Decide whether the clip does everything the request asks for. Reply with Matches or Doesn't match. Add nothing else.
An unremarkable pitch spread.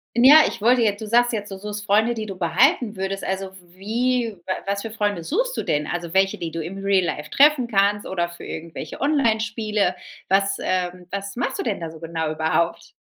Matches